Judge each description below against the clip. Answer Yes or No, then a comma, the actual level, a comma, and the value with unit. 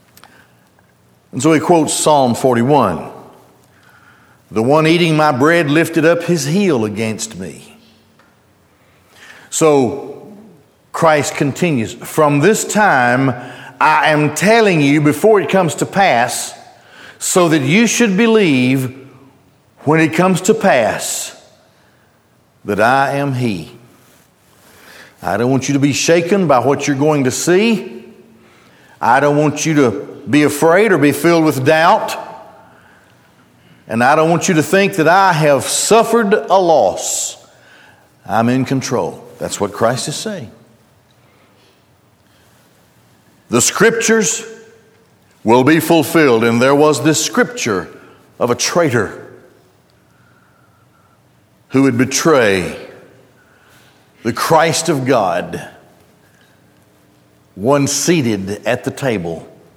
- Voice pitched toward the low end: No, medium, 150 Hz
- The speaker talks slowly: Yes, slow, 115 wpm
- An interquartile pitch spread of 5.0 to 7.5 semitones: No, average, 4.6 semitones